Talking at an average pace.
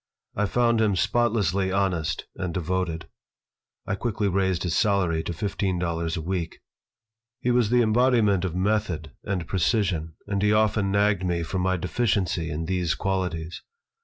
Yes: average, 155 wpm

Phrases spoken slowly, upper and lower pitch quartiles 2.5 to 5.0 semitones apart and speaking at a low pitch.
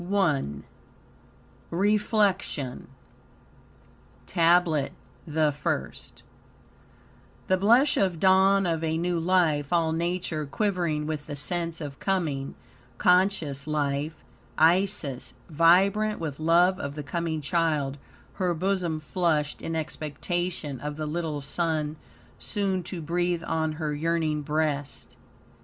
No: slow, 110 wpm; average, 3.1 semitones; medium, 165 Hz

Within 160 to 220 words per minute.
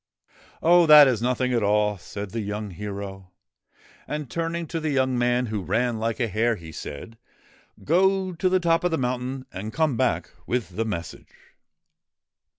Yes: average, 175 wpm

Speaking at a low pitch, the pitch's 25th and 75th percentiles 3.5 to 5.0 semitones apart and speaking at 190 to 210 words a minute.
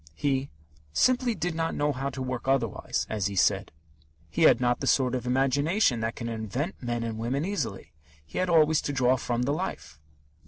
Yes: low, 130 Hz; average, 3.8 semitones; average, 195 wpm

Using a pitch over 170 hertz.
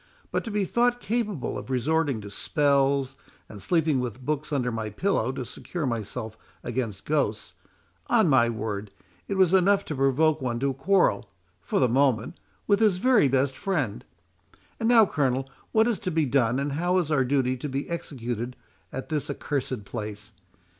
No: low, 135 Hz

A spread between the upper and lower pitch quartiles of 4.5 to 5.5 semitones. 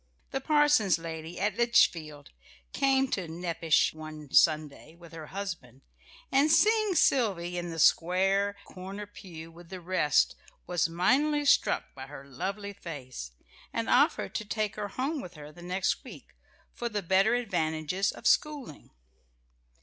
Yes: average, 5.2 semitones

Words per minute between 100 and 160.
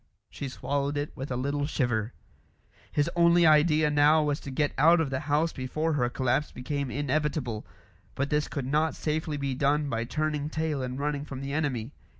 No: average, 185 wpm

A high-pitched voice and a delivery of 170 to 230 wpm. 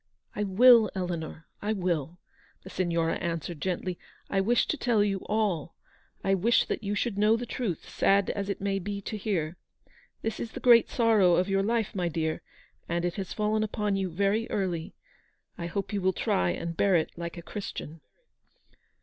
Yes: high, 195 Hz; average, 190 wpm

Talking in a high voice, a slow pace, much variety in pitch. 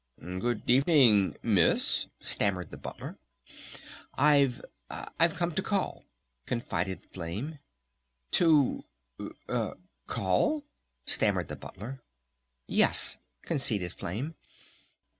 No: low, 120 Hz; slow, 85 wpm; wide, 8.1 semitones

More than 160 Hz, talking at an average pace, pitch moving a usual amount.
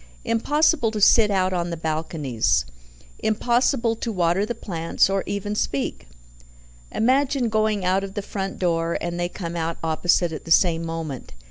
Yes: medium, 185 Hz; average, 160 wpm; average, 4.7 semitones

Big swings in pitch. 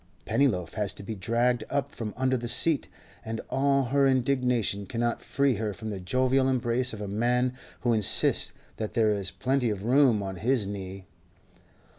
No: average, 3.7 semitones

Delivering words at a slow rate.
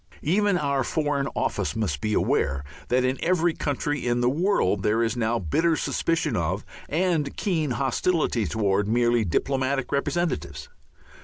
No: average, 145 wpm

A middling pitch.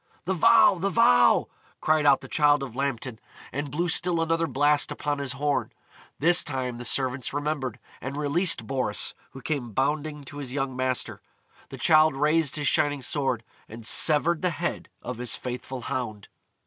Yes: medium, 145 Hz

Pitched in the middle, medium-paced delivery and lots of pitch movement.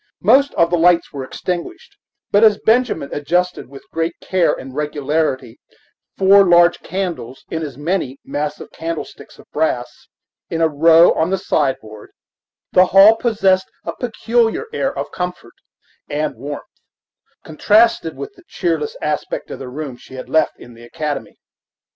No: medium, 165 Hz; average, 150 wpm; average, 4.9 semitones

